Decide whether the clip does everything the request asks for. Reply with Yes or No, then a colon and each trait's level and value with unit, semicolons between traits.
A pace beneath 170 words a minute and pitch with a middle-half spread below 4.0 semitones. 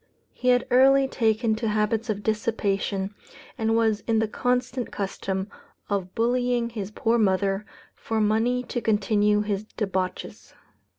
Yes: slow, 135 wpm; narrow, 2.5 semitones